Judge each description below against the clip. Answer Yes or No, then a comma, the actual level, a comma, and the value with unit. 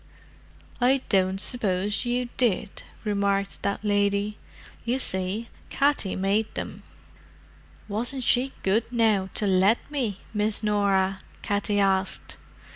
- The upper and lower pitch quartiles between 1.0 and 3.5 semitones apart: Yes, average, 3.0 semitones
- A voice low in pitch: No, high, 205 Hz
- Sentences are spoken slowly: Yes, slow, 115 wpm